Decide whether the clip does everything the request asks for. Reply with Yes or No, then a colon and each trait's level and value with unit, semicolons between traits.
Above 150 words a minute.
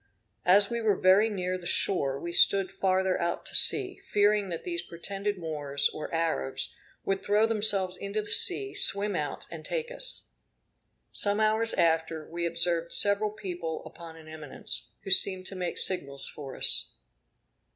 Yes: average, 160 wpm